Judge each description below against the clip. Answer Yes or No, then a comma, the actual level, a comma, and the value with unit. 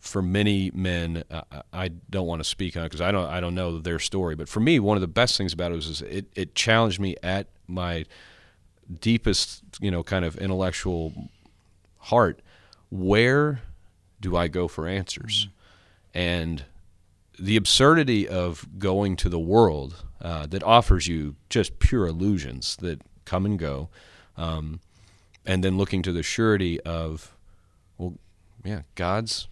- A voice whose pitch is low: Yes, very low, 90 Hz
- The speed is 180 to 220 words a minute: No, average, 165 wpm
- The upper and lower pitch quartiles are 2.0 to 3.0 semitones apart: Yes, average, 2.7 semitones